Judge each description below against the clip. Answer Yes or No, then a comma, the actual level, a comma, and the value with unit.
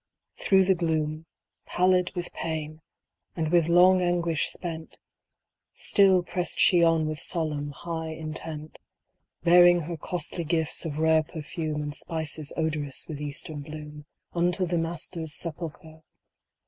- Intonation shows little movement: Yes, narrow, 2.1 semitones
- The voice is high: No, medium, 160 Hz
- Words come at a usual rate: No, slow, 130 wpm